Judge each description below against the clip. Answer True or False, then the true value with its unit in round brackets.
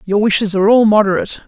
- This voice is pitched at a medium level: False (205 Hz)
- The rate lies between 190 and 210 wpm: True (205 wpm)